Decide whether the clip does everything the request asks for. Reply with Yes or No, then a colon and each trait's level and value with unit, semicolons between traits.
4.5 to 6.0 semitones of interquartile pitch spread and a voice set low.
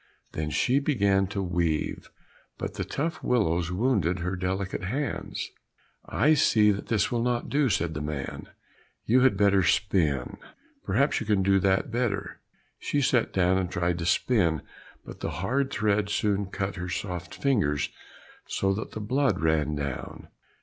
Yes: average, 5.2 semitones; very low, 95 Hz